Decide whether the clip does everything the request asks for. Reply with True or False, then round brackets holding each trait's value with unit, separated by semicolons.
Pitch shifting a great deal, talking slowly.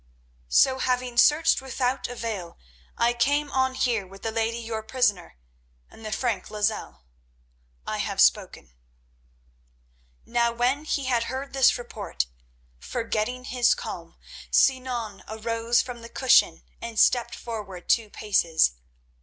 False (2.9 semitones; 130 wpm)